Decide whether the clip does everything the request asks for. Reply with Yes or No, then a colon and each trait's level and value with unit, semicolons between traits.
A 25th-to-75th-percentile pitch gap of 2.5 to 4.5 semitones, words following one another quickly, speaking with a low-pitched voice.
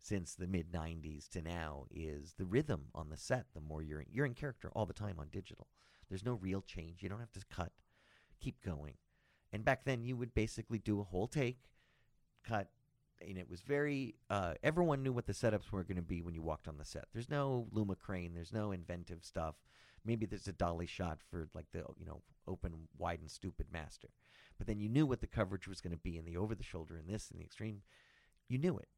No: average, 5.1 semitones; fast, 235 wpm; very low, 95 Hz